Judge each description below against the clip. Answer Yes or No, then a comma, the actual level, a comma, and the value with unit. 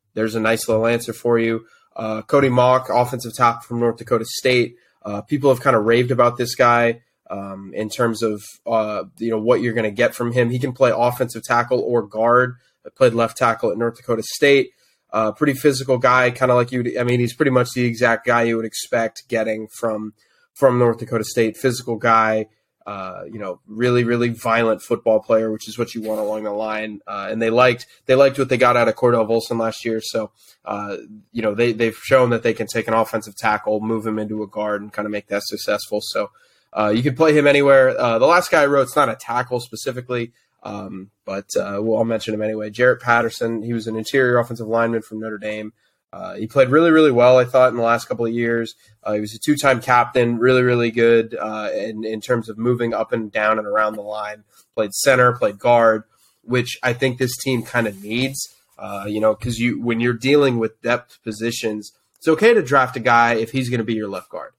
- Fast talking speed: Yes, fast, 230 wpm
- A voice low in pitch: Yes, low, 115 Hz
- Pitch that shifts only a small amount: Yes, narrow, 2.1 semitones